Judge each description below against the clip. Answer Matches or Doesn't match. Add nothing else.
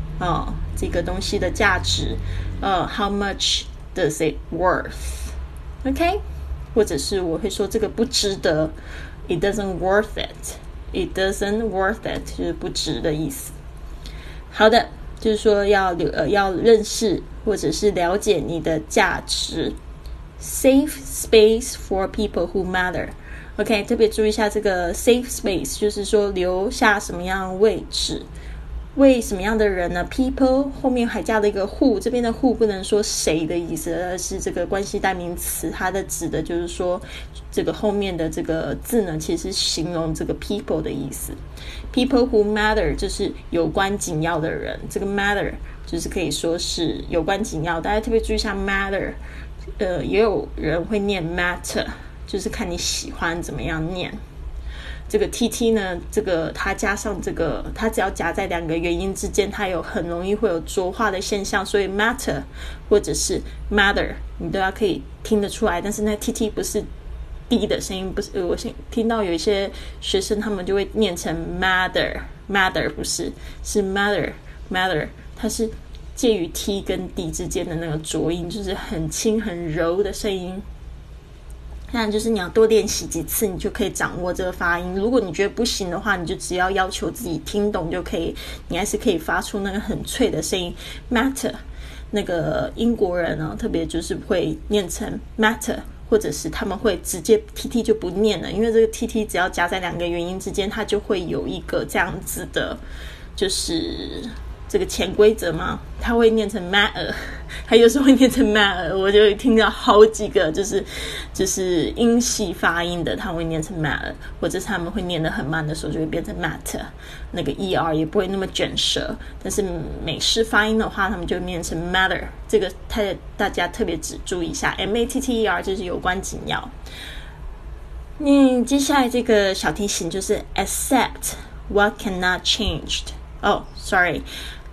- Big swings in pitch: Doesn't match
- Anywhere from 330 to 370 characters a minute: Matches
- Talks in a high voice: Matches